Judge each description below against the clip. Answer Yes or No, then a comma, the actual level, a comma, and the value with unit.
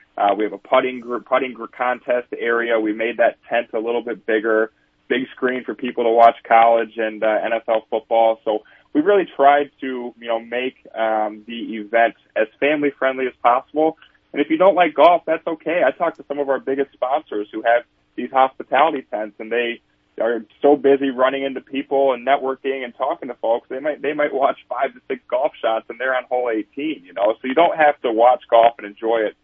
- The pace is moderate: No, fast, 220 wpm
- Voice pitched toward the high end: No, low, 125 Hz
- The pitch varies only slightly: No, average, 3.2 semitones